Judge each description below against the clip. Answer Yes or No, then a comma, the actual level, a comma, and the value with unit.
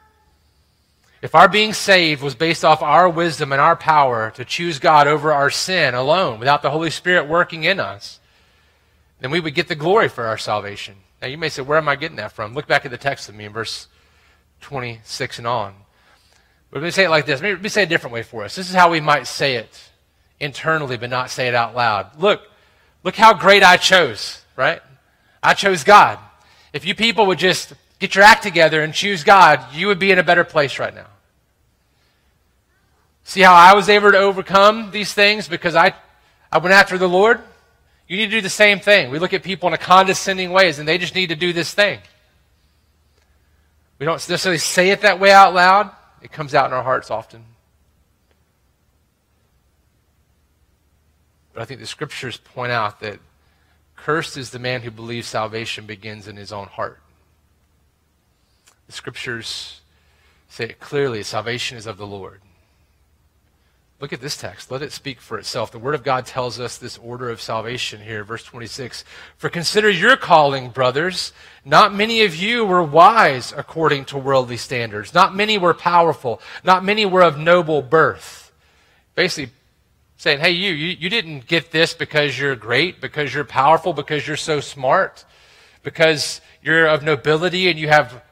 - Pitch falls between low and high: Yes, medium, 145 Hz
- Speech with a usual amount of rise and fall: No, wide, 8.6 semitones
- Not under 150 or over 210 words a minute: Yes, average, 190 wpm